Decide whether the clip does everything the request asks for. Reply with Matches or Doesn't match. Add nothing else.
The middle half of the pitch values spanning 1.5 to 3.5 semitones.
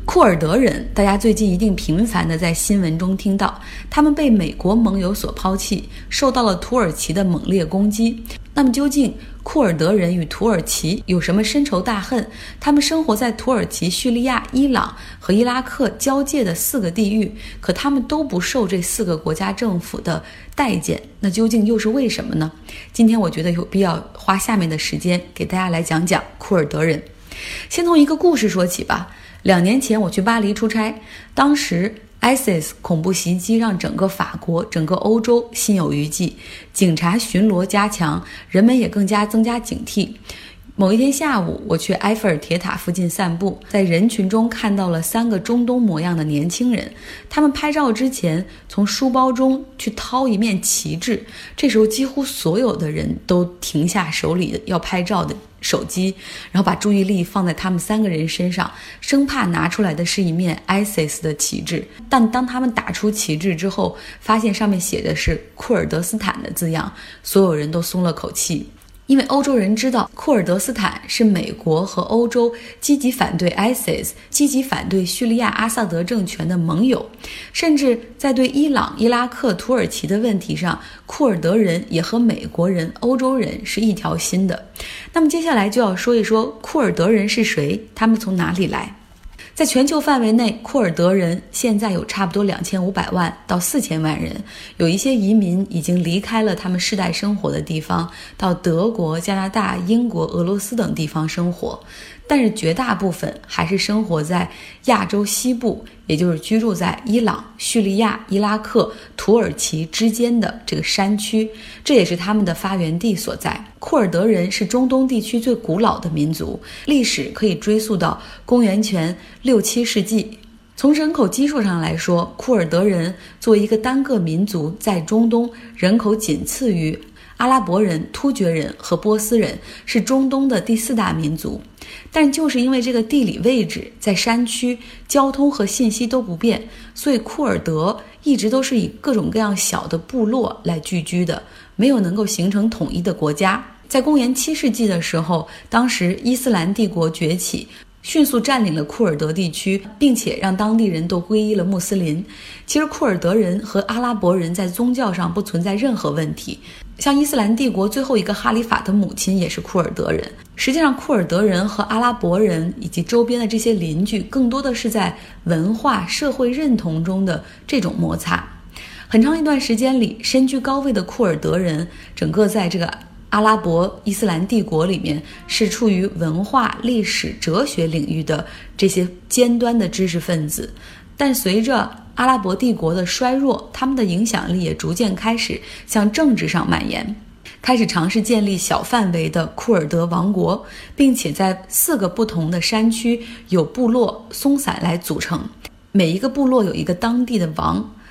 Doesn't match